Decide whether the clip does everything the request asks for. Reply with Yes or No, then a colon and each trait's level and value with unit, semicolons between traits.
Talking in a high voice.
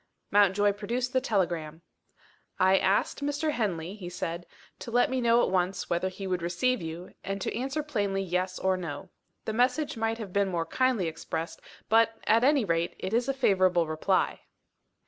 Yes: high, 195 Hz